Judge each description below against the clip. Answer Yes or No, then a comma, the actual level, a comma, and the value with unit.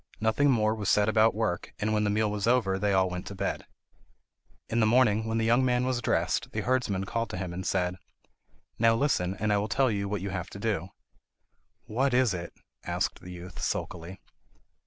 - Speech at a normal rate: No, fast, 210 wpm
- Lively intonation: No, average, 3.3 semitones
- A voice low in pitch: Yes, low, 105 Hz